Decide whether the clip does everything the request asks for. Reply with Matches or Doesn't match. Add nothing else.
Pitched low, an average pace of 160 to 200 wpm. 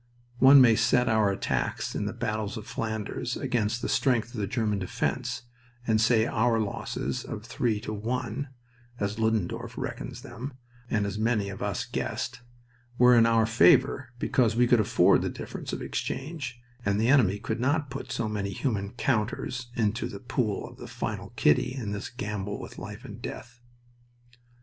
Matches